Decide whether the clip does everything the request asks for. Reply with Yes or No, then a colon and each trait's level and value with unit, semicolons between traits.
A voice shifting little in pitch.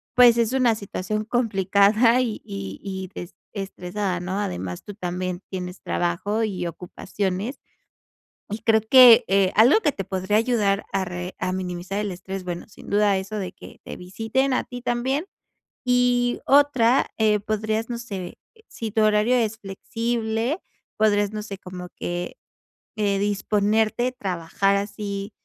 No: average, 3.3 semitones